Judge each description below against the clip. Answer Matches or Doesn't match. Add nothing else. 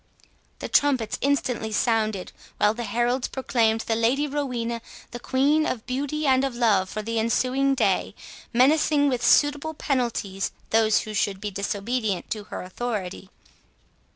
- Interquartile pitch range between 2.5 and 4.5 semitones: Matches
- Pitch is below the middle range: Doesn't match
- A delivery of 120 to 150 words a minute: Matches